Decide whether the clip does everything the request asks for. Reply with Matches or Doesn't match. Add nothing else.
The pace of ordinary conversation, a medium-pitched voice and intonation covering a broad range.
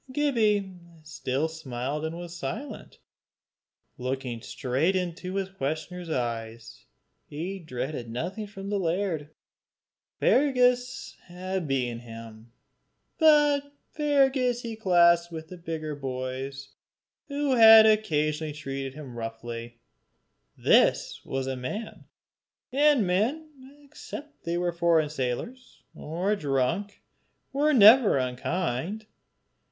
Doesn't match